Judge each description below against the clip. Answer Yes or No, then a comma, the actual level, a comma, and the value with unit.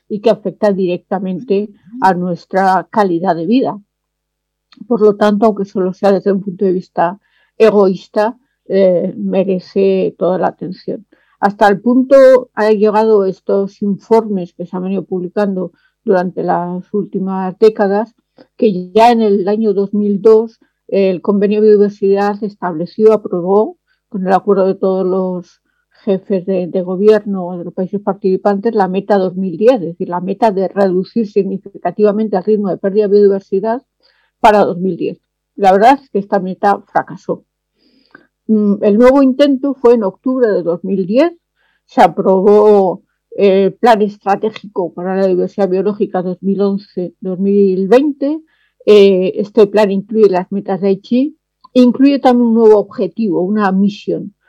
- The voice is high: Yes, high, 200 Hz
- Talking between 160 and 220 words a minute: No, average, 140 wpm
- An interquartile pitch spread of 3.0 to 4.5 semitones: No, narrow, 2.5 semitones